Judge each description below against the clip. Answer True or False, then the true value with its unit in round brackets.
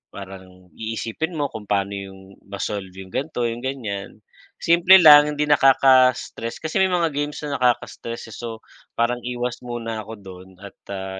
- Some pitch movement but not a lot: False (6.2 semitones)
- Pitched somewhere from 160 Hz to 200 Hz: False (115 Hz)